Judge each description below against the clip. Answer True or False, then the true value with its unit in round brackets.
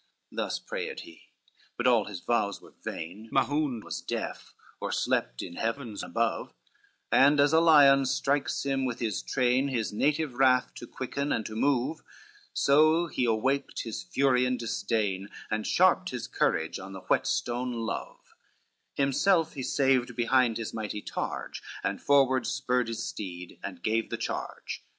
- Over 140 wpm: True (160 wpm)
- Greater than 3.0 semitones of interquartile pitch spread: True (4.0 semitones)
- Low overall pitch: True (125 Hz)